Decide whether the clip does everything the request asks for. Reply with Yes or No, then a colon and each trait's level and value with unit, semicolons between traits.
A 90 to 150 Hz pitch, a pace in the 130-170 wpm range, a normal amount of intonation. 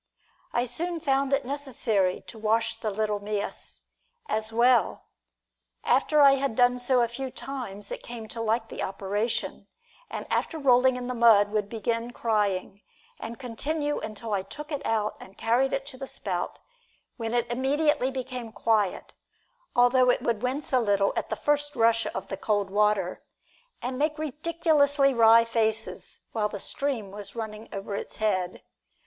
No: high, 235 Hz; average, 165 wpm; average, 4.0 semitones